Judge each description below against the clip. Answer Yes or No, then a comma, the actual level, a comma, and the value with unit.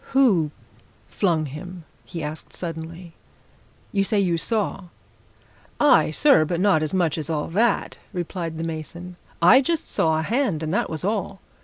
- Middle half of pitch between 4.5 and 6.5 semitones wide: No, average, 3.9 semitones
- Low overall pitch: No, medium, 175 Hz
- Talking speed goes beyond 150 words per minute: Yes, average, 160 wpm